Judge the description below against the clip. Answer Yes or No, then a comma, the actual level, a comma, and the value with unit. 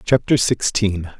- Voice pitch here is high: No, low, 105 Hz